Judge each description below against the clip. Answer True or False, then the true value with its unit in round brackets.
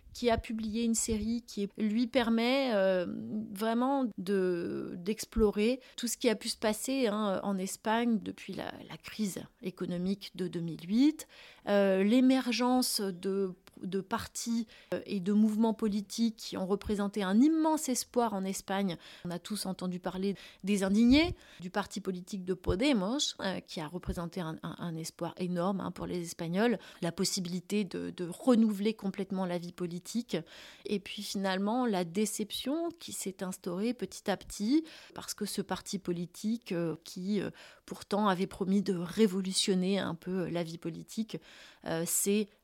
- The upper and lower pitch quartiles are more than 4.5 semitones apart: False (3.7 semitones)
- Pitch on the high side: True (200 Hz)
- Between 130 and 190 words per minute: True (150 wpm)